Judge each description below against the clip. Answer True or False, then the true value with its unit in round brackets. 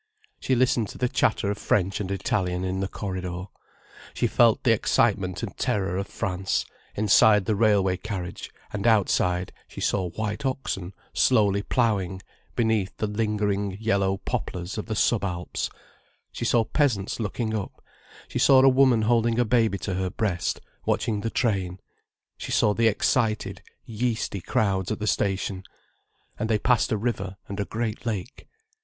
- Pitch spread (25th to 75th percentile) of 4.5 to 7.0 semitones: False (2.9 semitones)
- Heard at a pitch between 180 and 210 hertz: False (105 Hz)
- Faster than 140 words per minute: True (160 wpm)